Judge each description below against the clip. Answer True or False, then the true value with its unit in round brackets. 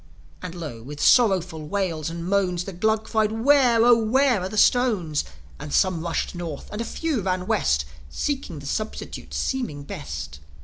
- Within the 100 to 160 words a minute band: False (170 wpm)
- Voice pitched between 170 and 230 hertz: True (185 Hz)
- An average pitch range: False (6.3 semitones)